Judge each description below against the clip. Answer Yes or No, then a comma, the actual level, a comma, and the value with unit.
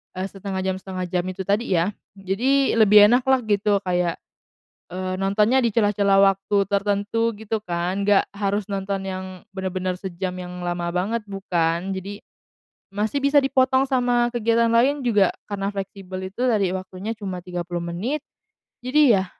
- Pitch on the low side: No, high, 195 Hz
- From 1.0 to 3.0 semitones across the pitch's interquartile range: No, average, 3.4 semitones